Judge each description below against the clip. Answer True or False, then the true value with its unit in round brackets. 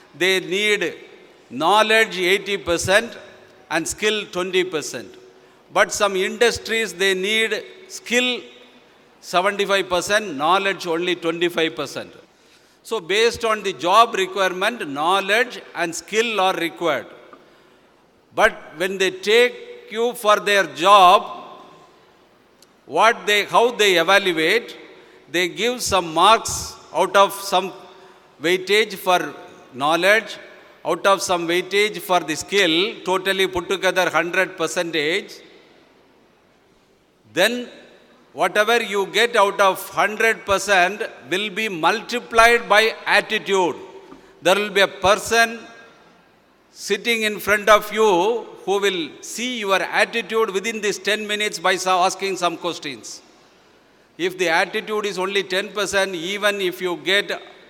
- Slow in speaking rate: False (115 wpm)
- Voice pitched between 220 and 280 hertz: False (200 Hz)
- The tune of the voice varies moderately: True (3.3 semitones)